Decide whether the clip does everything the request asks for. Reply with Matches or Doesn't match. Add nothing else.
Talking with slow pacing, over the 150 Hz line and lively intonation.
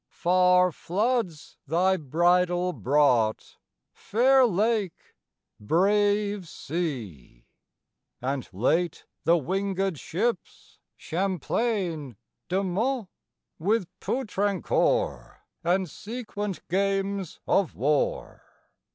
Doesn't match